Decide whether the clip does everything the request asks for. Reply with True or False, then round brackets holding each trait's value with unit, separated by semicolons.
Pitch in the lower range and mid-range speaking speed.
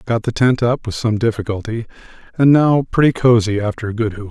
True (115 Hz; 195 wpm)